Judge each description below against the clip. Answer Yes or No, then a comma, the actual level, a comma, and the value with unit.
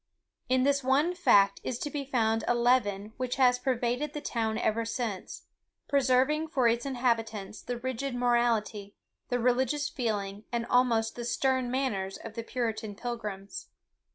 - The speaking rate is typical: Yes, average, 155 wpm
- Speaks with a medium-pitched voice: No, high, 240 Hz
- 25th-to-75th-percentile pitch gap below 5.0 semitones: Yes, average, 2.7 semitones